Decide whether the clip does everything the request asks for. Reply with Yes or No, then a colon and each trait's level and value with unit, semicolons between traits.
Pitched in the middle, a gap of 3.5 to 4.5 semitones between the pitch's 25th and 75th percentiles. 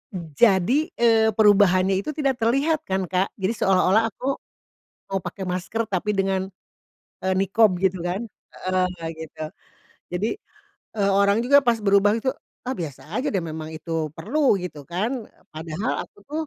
No: high, 195 Hz; average, 3.8 semitones